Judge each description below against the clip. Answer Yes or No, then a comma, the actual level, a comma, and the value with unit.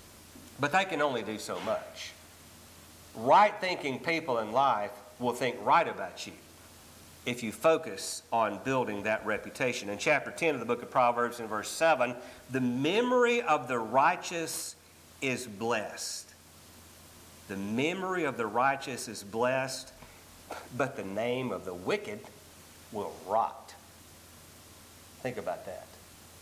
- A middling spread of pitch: No, wide, 7.4 semitones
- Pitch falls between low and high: No, low, 115 Hz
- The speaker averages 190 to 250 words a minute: No, slow, 135 wpm